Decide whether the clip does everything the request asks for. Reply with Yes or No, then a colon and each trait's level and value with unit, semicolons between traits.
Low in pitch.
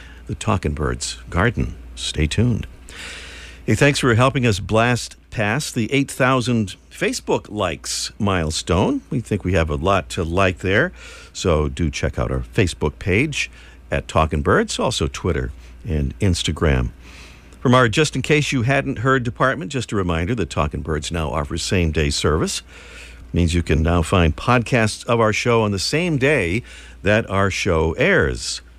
Yes: very low, 90 Hz